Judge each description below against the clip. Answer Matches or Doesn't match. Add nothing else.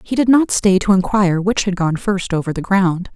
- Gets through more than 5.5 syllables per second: Doesn't match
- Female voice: Matches